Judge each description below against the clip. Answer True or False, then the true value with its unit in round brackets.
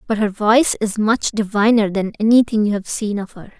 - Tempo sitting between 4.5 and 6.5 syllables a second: True (5.5 syllables/s)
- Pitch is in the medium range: False (215 Hz)